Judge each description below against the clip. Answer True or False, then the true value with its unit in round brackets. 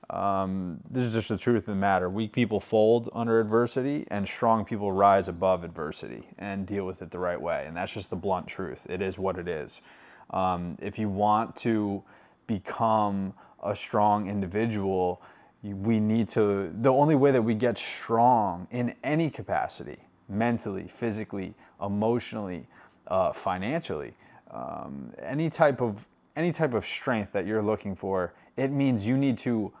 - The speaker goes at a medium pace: True (165 wpm)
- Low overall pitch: True (105 Hz)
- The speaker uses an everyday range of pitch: True (3.2 semitones)